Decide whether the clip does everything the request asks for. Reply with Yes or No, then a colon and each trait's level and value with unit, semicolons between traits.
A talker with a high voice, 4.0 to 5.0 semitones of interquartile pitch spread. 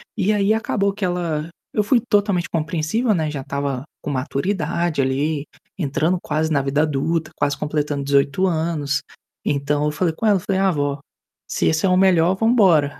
No: medium, 160 Hz; average, 4.6 semitones